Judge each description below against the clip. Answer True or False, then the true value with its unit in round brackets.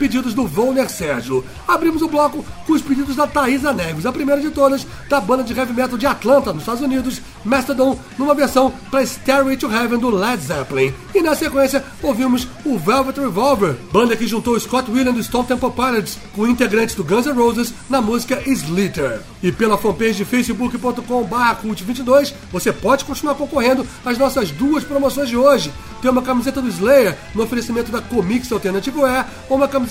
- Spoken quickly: False (185 wpm)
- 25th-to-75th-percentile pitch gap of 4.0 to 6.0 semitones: False (3.0 semitones)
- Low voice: False (255 Hz)